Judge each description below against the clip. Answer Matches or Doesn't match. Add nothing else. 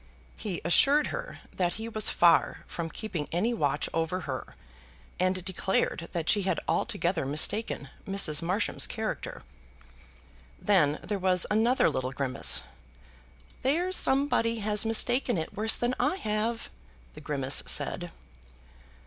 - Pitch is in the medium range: Doesn't match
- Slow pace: Matches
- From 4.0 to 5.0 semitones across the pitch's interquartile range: Doesn't match